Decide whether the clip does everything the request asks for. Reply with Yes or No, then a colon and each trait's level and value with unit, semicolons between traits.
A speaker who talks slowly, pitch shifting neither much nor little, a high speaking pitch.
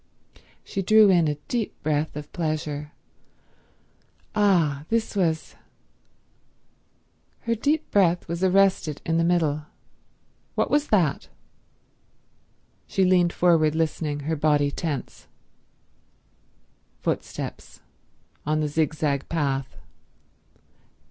No: slow, 95 wpm; average, 3.9 semitones; medium, 160 Hz